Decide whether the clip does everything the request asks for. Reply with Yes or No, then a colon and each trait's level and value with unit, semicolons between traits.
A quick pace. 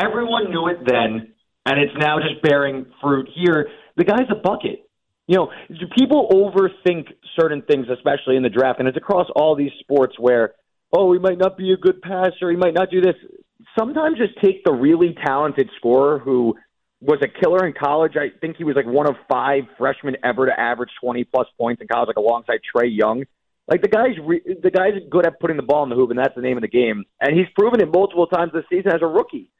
Yes: fast, 225 wpm